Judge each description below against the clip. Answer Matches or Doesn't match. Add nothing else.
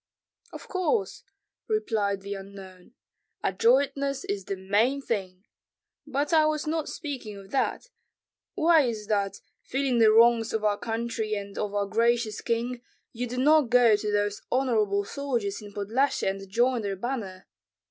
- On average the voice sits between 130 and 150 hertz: Doesn't match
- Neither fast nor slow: Matches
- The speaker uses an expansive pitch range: Doesn't match